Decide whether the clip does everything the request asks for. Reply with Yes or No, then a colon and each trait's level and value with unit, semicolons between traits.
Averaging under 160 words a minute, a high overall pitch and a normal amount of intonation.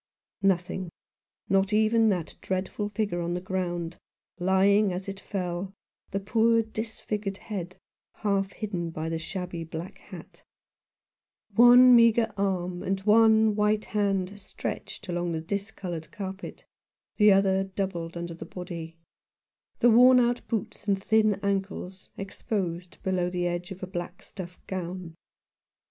Yes: average, 140 wpm; high, 195 Hz; average, 3.0 semitones